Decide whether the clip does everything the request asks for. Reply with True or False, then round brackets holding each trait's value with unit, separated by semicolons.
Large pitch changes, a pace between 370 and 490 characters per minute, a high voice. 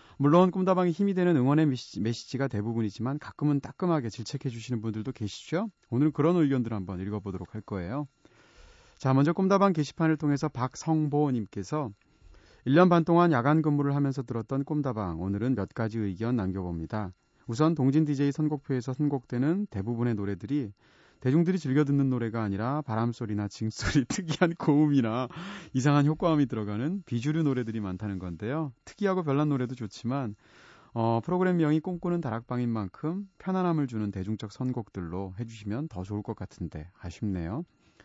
False (5.8 semitones; 385 characters per minute; 130 Hz)